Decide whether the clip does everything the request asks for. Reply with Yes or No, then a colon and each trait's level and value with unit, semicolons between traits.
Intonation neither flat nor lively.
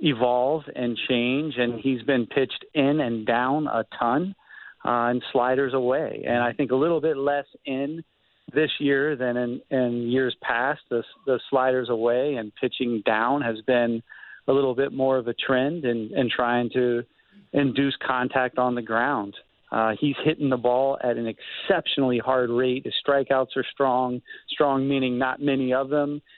No: narrow, 2.3 semitones